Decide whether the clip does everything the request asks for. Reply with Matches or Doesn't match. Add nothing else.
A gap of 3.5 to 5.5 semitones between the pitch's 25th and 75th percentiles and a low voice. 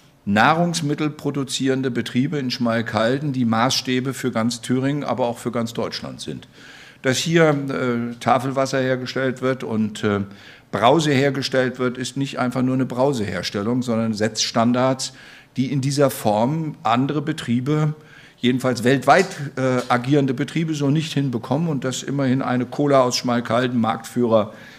Doesn't match